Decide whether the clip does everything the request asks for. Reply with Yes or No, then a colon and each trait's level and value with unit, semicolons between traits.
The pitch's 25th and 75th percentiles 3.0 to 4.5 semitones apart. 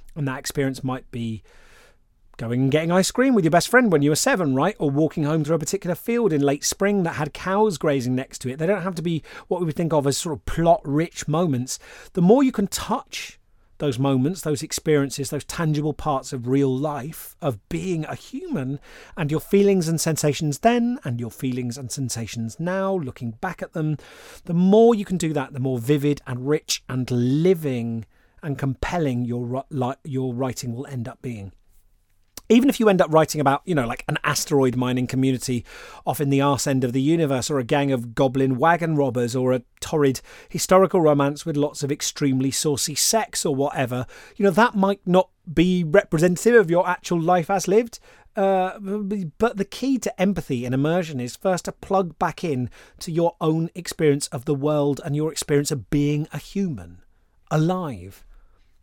No: average, 5.3 semitones